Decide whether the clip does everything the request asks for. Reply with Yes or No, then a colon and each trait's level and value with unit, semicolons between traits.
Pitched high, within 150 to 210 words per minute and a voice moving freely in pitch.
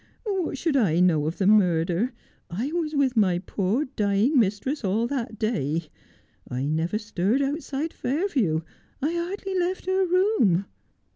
Yes: high, 230 Hz; average, 160 wpm; wide, 9.0 semitones